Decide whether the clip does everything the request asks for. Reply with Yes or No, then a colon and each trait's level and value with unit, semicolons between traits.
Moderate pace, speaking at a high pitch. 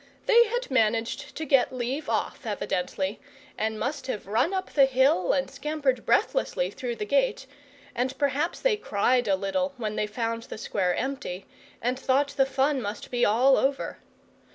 Yes: average, 170 wpm; very high, 260 Hz